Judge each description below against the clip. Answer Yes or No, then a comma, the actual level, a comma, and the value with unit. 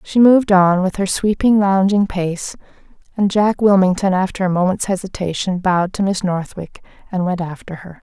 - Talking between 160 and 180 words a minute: Yes, average, 170 wpm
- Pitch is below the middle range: No, high, 190 Hz